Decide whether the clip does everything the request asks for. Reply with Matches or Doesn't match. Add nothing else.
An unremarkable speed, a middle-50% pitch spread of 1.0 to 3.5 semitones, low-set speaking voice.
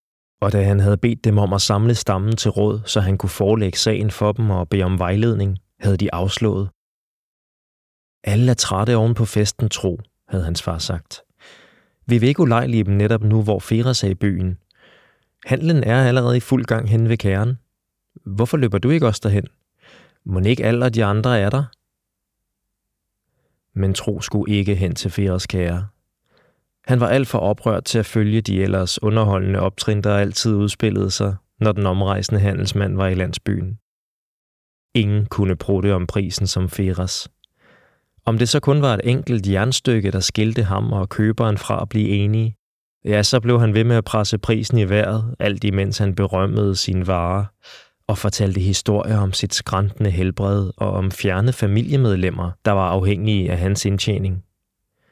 Matches